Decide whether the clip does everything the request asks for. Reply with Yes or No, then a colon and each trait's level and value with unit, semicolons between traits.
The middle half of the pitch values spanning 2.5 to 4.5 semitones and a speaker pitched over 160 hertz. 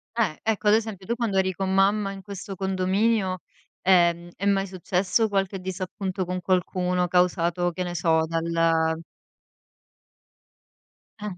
No: narrow, 2.0 semitones; medium, 185 Hz